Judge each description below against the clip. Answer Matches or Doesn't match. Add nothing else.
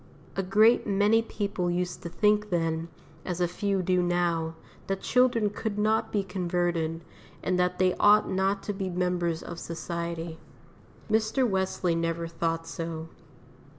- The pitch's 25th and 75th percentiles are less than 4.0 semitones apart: Matches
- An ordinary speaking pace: Matches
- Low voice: Doesn't match